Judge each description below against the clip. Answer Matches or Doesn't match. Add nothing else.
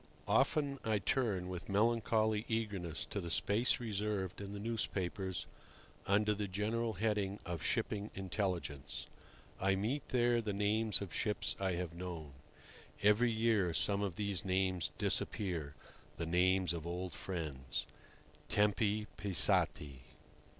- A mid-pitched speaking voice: Doesn't match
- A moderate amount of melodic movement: Matches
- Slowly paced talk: Matches